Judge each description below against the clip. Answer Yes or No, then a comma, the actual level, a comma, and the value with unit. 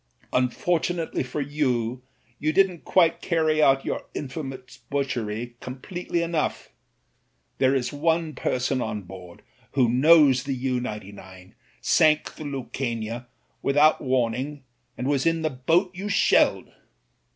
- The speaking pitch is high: No, low, 135 Hz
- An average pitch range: Yes, average, 4.0 semitones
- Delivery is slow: Yes, slow, 125 wpm